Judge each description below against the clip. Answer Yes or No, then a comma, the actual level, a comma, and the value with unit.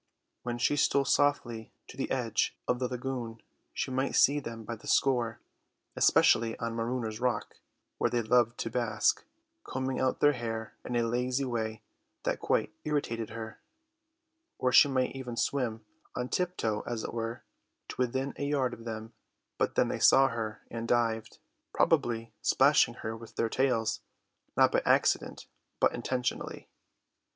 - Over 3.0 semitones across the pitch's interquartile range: No, narrow, 2.5 semitones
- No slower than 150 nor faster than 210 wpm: Yes, average, 160 wpm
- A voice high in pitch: No, low, 120 Hz